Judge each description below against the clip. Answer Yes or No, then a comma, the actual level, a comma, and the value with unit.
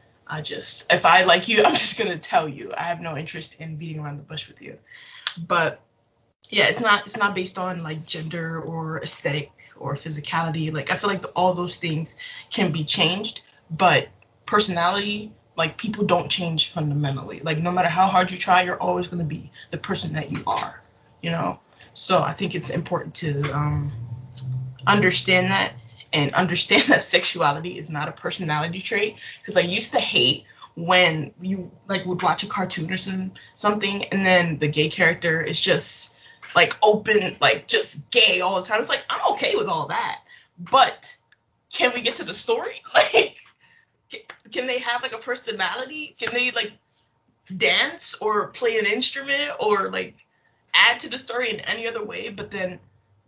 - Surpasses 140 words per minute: Yes, average, 180 wpm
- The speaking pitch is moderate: Yes, medium, 180 Hz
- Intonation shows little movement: No, average, 5.1 semitones